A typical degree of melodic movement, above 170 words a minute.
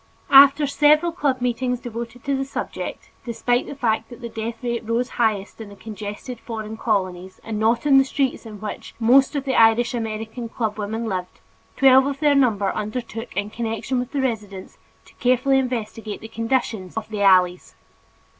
Yes: average, 3.3 semitones; average, 180 wpm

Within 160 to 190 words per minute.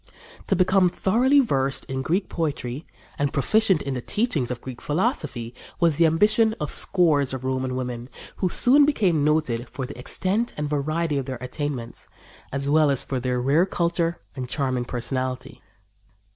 Yes: average, 165 wpm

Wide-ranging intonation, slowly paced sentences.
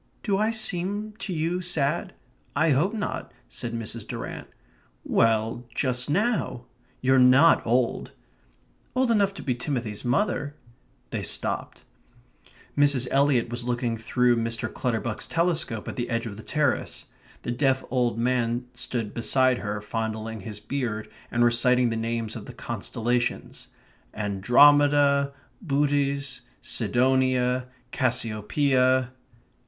No: average, 3.7 semitones; slow, 125 wpm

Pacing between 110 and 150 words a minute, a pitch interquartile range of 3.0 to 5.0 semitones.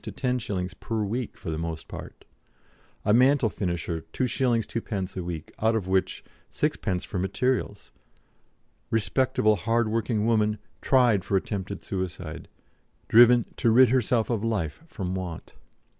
Yes: average, 140 wpm; average, 4.1 semitones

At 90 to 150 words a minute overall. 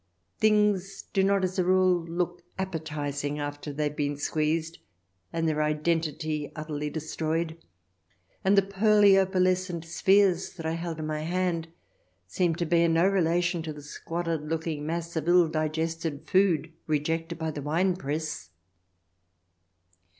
Yes: average, 140 wpm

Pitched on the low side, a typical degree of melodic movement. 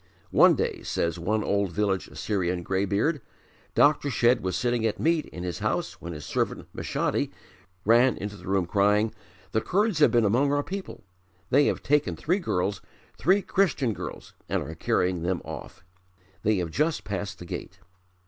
No: low, 105 Hz; wide, 7.3 semitones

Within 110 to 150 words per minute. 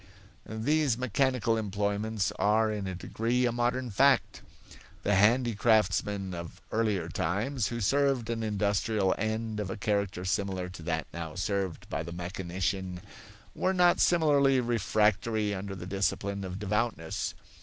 Yes: slow, 135 wpm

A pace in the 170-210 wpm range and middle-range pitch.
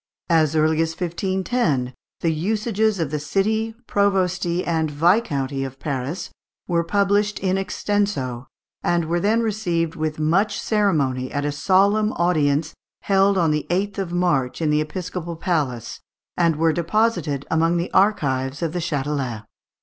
No: average, 150 wpm; medium, 170 Hz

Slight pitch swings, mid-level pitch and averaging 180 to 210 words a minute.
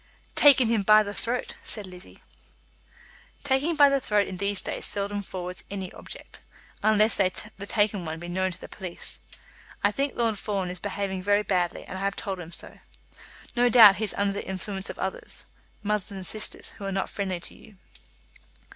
No: narrow, 2.2 semitones; high, 200 Hz; average, 190 wpm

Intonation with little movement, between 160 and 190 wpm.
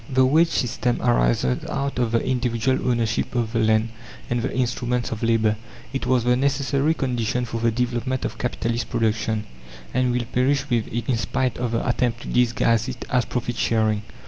Yes: narrow, 2.0 semitones; average, 185 wpm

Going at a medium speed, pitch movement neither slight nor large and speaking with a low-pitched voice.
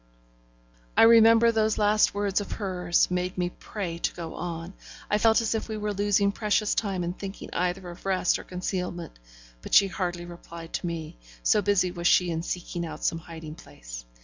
No: average, 190 wpm; average, 3.1 semitones; medium, 180 Hz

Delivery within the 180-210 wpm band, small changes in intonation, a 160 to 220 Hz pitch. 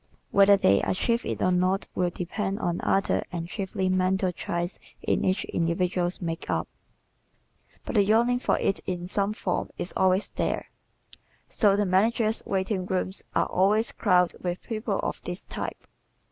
No: average, 155 wpm; narrow, 2.1 semitones; high, 190 Hz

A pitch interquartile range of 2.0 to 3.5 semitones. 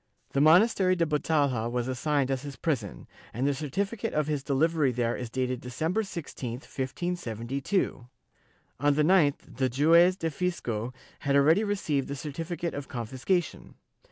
No: average, 4.5 semitones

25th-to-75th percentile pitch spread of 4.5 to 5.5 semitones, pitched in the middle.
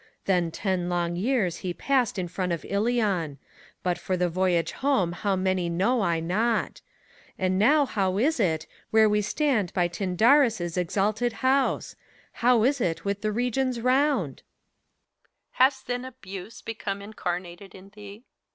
No: average, 5.2 semitones; high, 200 Hz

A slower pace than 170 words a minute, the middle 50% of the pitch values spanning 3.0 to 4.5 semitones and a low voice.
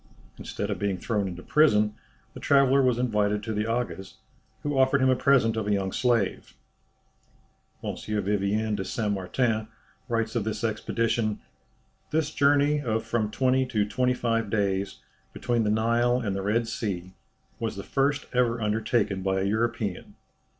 Yes: average, 160 wpm; average, 3.3 semitones; low, 110 Hz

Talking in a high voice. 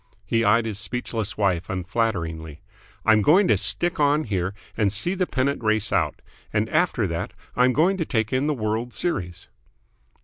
No: low, 110 Hz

